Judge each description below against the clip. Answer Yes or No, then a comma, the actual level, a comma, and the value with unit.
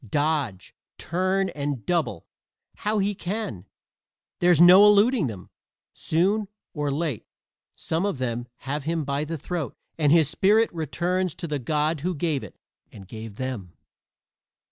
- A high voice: No, medium, 160 Hz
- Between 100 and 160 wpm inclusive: Yes, average, 145 wpm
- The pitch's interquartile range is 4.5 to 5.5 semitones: Yes, average, 5.1 semitones